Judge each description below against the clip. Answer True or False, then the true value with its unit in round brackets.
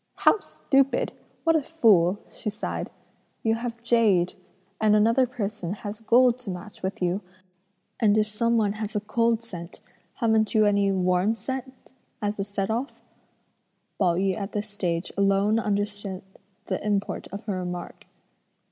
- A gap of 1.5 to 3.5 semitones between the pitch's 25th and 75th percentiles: True (2.8 semitones)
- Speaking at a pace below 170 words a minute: True (150 wpm)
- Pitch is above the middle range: True (210 Hz)